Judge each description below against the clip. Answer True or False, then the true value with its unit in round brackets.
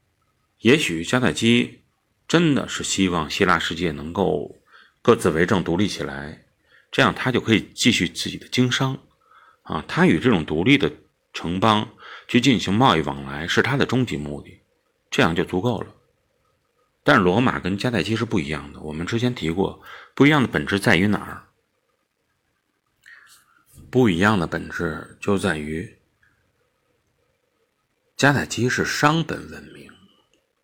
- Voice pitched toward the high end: False (95 Hz)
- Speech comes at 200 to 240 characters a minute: True (220 characters per minute)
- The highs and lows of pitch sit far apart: True (6.0 semitones)